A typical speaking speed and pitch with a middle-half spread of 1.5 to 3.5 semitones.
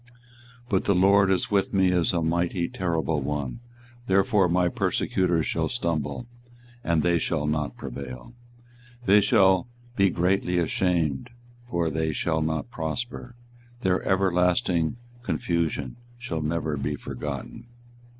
No: slow, 130 wpm; average, 3.2 semitones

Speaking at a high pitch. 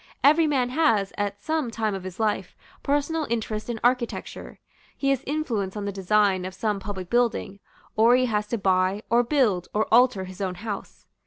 Yes: high, 215 Hz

